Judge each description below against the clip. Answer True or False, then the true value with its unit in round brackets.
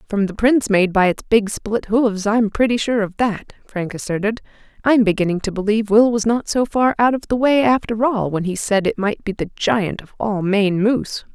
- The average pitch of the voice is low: False (215 Hz)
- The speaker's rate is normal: False (225 wpm)